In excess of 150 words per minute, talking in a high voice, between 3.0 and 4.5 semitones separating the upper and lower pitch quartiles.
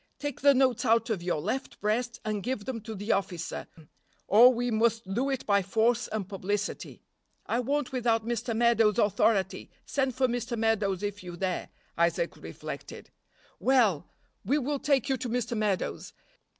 Yes: average, 165 wpm; high, 225 Hz; average, 3.5 semitones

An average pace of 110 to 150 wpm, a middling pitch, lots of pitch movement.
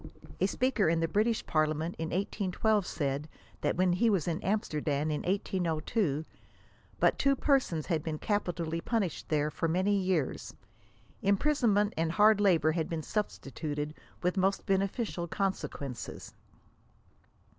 No: slow, 135 wpm; medium, 180 Hz; average, 4.5 semitones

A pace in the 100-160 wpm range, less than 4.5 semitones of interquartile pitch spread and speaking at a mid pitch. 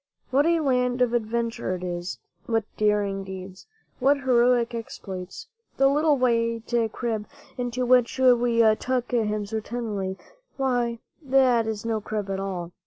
No: average, 145 wpm; average, 3.3 semitones; high, 235 Hz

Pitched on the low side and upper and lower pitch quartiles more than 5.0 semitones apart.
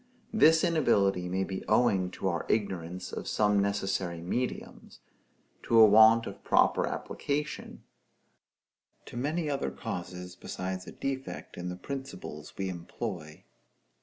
Yes: low, 100 Hz; wide, 5.5 semitones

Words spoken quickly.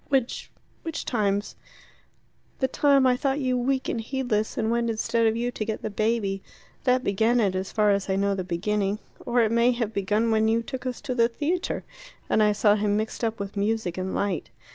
Yes: fast, 210 wpm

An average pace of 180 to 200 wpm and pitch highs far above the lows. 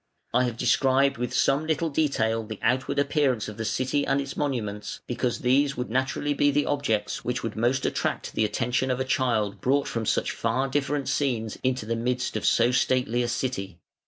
No: average, 195 wpm; average, 3.2 semitones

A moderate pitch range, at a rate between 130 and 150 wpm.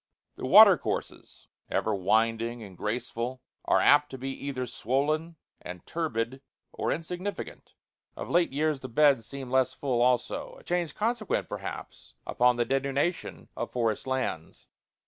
Yes: average, 4.1 semitones; average, 140 wpm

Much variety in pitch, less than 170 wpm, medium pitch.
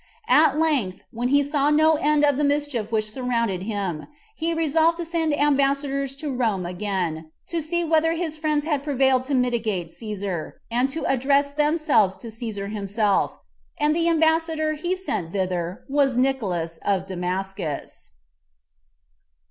No: wide, 7.1 semitones; average, 150 wpm; very high, 270 Hz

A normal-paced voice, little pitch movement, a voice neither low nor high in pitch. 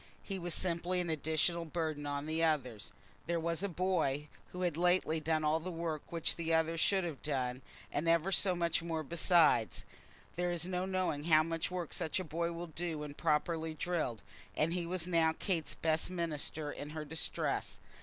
Yes: average, 190 wpm; narrow, 2.2 semitones; medium, 165 Hz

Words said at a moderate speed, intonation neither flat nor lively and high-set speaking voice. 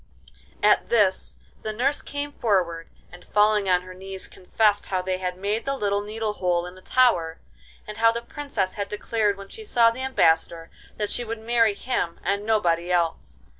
Yes: average, 185 wpm; average, 3.9 semitones; high, 205 Hz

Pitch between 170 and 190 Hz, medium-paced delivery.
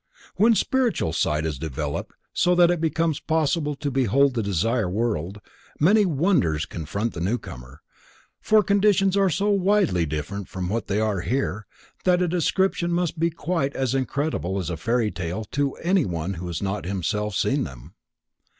No: low, 125 Hz; average, 170 wpm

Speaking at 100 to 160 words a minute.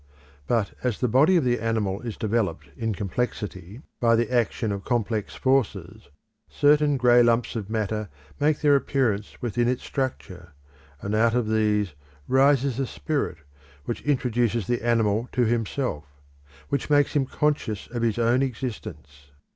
Yes: average, 150 wpm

